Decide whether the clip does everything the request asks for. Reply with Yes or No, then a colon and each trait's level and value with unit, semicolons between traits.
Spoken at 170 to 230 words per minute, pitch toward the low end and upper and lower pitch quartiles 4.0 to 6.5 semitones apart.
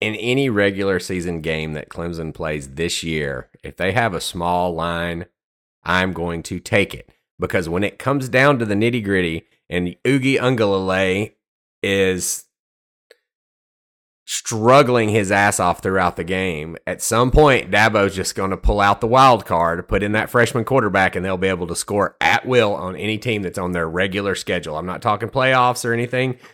Yes: average, 180 wpm; very low, 95 Hz; average, 5.2 semitones